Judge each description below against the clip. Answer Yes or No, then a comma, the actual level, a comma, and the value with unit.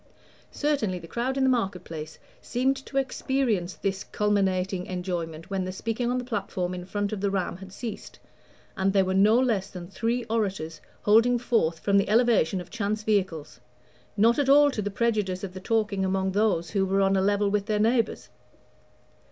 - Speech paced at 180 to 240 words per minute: Yes, average, 190 wpm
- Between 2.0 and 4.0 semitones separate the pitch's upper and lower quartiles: Yes, average, 3.6 semitones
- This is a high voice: Yes, high, 200 Hz